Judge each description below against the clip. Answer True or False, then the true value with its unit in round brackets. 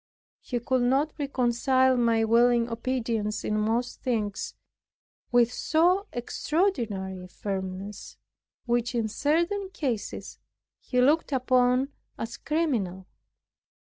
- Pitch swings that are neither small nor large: True (3.4 semitones)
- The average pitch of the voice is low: False (245 Hz)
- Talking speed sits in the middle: False (105 wpm)